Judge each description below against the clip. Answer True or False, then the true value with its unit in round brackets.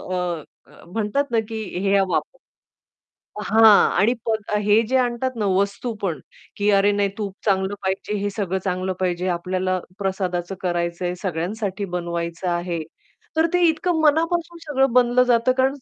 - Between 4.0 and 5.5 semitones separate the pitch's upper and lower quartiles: True (4.6 semitones)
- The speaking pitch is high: True (200 Hz)